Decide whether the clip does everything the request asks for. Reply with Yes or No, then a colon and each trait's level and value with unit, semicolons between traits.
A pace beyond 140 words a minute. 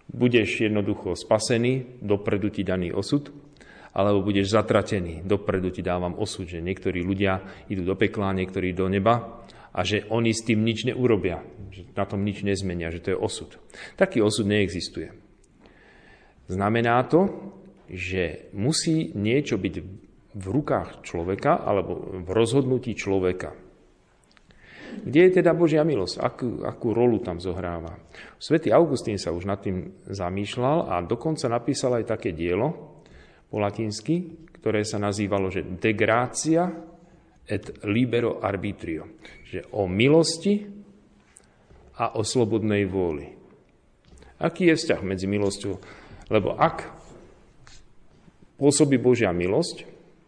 No: average, 125 wpm